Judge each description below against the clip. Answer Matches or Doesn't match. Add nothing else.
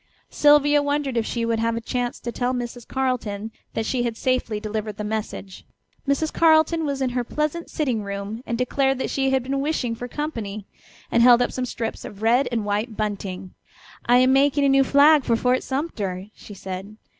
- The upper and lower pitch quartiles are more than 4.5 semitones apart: Doesn't match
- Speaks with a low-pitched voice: Doesn't match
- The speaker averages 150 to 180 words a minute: Doesn't match